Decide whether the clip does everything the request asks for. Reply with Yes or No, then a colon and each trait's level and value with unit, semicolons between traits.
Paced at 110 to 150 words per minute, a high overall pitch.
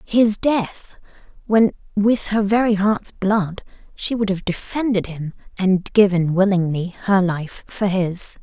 Yes: average, 145 wpm; high, 195 Hz